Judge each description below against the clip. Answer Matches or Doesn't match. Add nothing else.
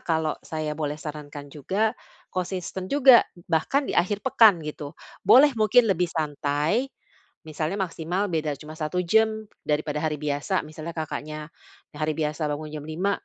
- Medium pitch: Matches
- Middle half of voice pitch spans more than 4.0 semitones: Matches